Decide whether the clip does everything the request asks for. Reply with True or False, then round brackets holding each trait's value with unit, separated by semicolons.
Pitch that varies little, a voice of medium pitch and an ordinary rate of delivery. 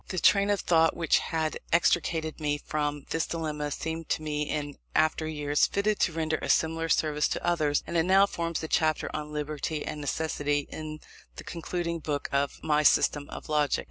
True (1.8 semitones; 155 Hz; 190 wpm)